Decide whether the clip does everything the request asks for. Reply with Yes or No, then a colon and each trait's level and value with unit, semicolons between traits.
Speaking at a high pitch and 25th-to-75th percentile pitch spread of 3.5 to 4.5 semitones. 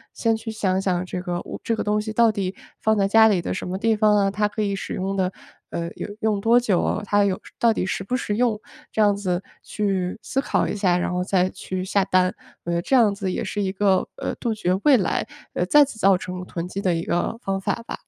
No: high, 200 Hz; average, 2.9 semitones